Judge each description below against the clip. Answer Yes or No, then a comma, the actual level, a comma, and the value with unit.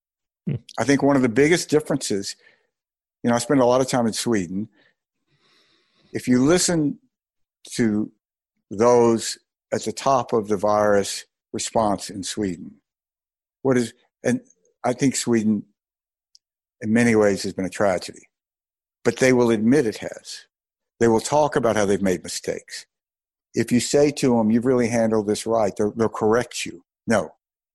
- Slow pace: No, average, 155 wpm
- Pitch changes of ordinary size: Yes, average, 4.5 semitones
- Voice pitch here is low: Yes, low, 120 Hz